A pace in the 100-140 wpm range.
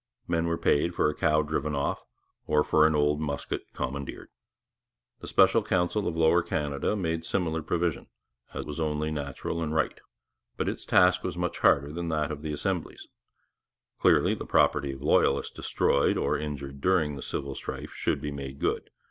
No: average, 175 wpm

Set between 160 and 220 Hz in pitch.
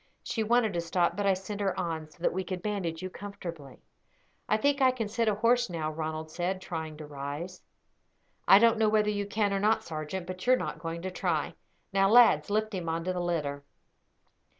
Yes: medium, 185 Hz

